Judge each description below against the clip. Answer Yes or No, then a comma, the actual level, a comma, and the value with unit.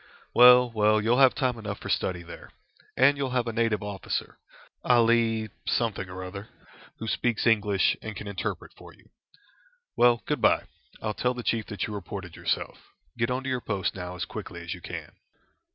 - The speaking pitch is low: Yes, low, 110 Hz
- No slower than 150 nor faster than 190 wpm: Yes, average, 185 wpm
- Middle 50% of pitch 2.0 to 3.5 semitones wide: Yes, average, 3.2 semitones